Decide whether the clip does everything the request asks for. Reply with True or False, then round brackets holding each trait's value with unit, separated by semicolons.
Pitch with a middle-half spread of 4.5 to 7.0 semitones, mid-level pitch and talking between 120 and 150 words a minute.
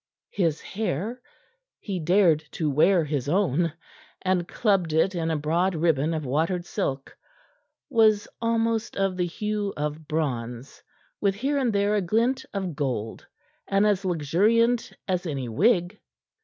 True (5.2 semitones; 180 Hz; 140 wpm)